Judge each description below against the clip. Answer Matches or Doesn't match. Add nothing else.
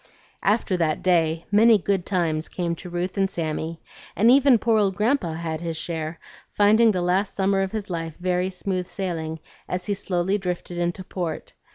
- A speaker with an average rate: Matches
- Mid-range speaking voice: Matches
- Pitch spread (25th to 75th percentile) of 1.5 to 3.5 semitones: Matches